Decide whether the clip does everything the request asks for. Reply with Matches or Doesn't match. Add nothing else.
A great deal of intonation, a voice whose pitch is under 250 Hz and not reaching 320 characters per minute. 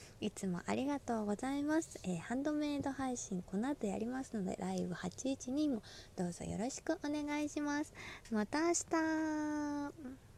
Doesn't match